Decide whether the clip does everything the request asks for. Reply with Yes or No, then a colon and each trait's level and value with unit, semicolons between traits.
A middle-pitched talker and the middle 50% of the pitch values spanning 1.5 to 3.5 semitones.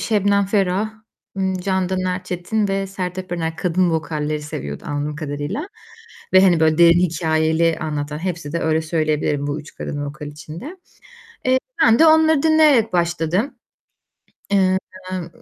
No: medium, 175 Hz; average, 4.0 semitones